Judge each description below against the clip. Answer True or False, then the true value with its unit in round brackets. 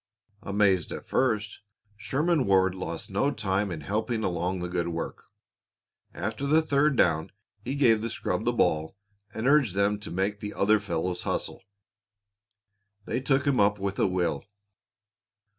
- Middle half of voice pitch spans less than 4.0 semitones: False (5.1 semitones)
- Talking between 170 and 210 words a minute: False (155 wpm)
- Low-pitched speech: True (100 Hz)